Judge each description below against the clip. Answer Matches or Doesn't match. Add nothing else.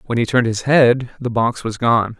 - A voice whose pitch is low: Matches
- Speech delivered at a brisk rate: Matches